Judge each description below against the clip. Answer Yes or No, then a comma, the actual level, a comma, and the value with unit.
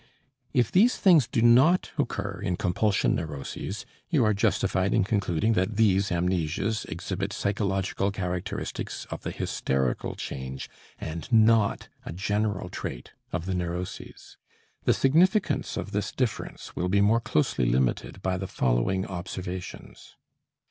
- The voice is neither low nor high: No, very low, 95 Hz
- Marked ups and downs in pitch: No, average, 3.7 semitones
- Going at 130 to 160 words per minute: Yes, slow, 135 wpm